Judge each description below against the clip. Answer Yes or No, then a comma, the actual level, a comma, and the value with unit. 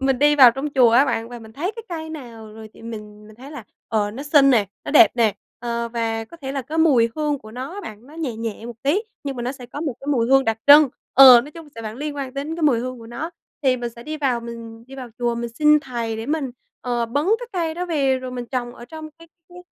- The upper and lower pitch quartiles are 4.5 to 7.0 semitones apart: No, average, 4.1 semitones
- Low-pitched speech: No, very high, 255 Hz